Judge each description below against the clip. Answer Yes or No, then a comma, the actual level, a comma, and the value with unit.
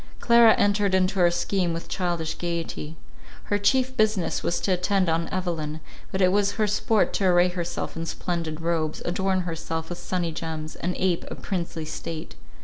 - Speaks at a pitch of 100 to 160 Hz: No, medium, 175 Hz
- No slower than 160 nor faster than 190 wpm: Yes, average, 175 wpm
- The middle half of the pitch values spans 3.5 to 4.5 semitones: No, average, 2.8 semitones